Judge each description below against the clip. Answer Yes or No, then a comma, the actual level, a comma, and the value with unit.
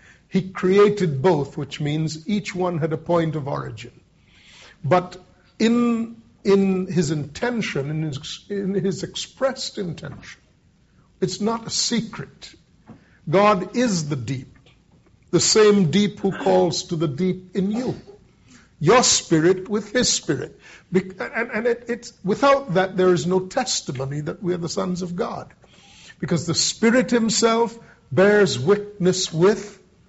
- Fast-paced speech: No, average, 140 wpm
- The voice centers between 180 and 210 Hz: Yes, medium, 185 Hz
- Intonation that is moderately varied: Yes, average, 3.8 semitones